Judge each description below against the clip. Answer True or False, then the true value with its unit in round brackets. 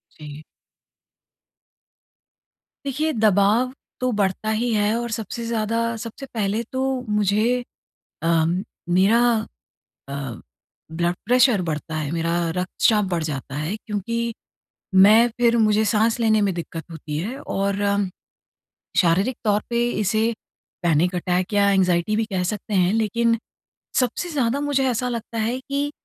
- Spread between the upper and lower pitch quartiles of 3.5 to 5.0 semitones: True (4.4 semitones)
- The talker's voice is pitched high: True (210 Hz)